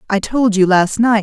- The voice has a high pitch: Yes, high, 210 Hz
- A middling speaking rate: No, fast, 245 wpm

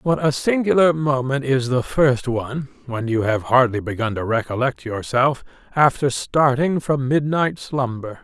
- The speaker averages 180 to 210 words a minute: No, average, 155 wpm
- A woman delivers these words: No, male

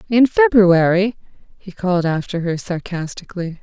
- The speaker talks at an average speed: No, slow, 115 wpm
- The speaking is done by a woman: Yes, female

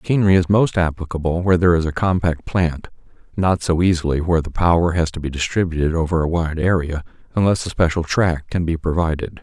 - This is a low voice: Yes, very low, 85 Hz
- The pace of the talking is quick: No, average, 195 wpm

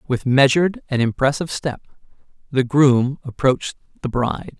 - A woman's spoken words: No, male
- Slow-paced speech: Yes, slow, 130 wpm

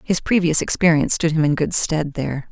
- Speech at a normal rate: No, fast, 215 wpm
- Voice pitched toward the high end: No, medium, 160 Hz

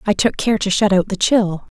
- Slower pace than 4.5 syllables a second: No, 5.1 syllables/s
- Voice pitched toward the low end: No, high, 205 Hz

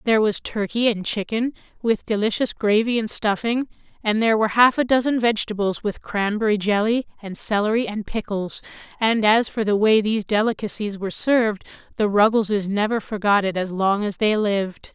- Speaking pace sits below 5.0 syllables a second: No, 5.5 syllables/s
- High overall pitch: Yes, high, 215 Hz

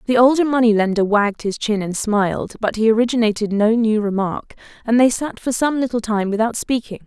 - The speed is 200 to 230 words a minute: Yes, fast, 205 wpm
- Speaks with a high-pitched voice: Yes, high, 225 Hz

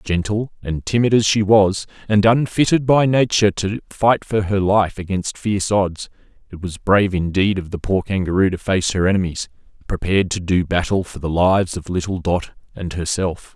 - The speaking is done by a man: Yes, male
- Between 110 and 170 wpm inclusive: No, average, 185 wpm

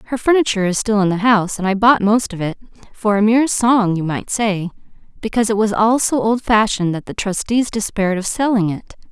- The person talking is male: No, female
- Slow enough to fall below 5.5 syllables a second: No, 6.0 syllables/s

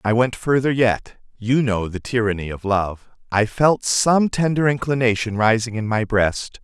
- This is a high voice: No, low, 115 Hz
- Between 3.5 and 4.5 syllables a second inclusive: Yes, 4.4 syllables/s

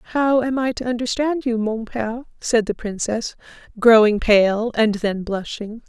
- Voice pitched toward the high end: Yes, high, 230 Hz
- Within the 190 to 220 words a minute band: No, average, 165 wpm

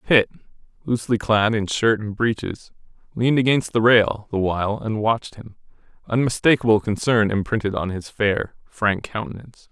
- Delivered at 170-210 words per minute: No, average, 150 wpm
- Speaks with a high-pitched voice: No, low, 110 Hz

